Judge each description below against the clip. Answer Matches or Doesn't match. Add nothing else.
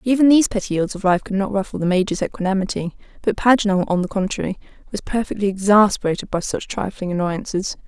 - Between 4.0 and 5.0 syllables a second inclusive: Doesn't match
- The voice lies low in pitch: Doesn't match